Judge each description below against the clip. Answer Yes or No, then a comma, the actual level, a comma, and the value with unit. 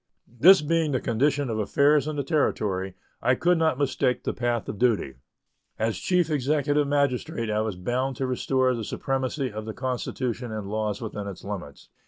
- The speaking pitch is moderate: No, low, 125 Hz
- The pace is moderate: Yes, average, 180 wpm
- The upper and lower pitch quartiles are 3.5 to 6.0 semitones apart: Yes, average, 4.7 semitones